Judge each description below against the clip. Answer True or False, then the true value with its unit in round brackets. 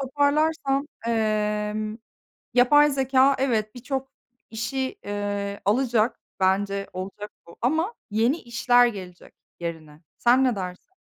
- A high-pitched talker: True (230 Hz)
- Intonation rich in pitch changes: False (4.7 semitones)